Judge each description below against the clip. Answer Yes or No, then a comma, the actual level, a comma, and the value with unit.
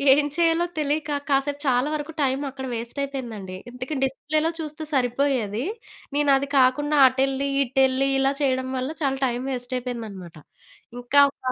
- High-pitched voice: Yes, very high, 270 Hz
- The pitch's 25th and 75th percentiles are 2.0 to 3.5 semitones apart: Yes, narrow, 2.4 semitones